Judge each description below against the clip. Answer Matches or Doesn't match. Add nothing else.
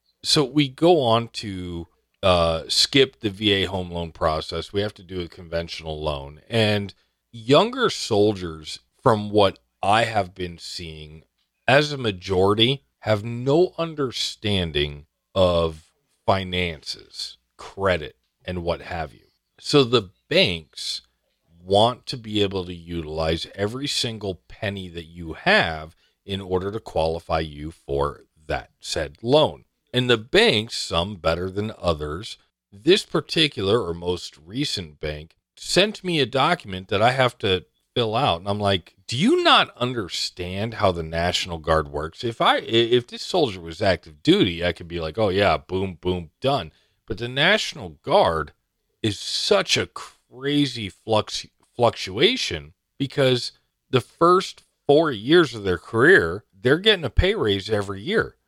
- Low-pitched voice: Matches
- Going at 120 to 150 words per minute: Matches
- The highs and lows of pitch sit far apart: Matches